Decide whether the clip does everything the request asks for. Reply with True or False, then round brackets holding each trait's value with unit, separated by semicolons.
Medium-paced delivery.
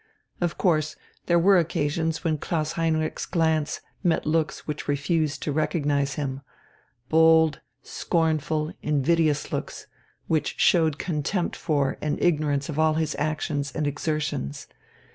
False (125 wpm)